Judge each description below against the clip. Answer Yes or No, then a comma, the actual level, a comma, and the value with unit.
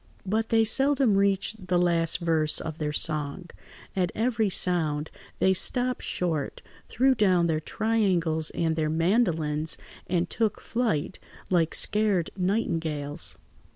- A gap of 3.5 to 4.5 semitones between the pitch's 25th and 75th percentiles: No, average, 5.2 semitones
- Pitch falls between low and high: Yes, medium, 180 Hz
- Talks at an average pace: No, slow, 125 wpm